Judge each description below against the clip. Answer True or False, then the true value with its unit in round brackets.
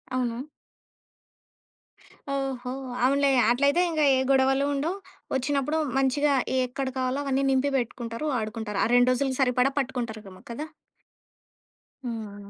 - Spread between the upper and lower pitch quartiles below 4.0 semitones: True (2.5 semitones)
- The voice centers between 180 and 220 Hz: False (260 Hz)